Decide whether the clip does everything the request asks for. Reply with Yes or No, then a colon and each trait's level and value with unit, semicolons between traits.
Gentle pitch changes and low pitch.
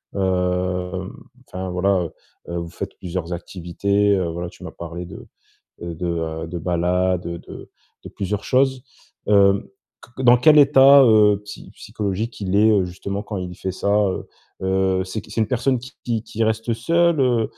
No: average, 3.7 semitones; very low, 95 Hz